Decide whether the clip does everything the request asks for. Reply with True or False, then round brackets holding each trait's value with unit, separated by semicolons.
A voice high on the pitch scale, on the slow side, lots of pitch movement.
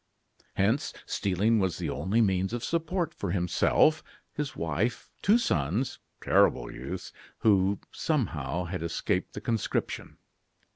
False (100 Hz; 125 wpm; 6.6 semitones)